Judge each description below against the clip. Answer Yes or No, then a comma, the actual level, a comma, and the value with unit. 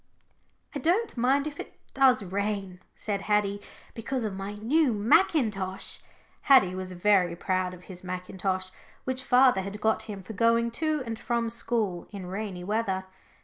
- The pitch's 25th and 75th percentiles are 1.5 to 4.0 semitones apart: No, average, 4.4 semitones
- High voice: Yes, high, 210 Hz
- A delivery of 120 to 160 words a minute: Yes, average, 155 wpm